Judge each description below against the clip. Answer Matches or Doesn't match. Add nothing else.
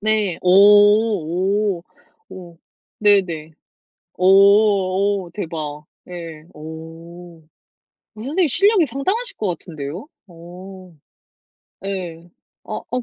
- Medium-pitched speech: Matches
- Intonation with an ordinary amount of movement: Matches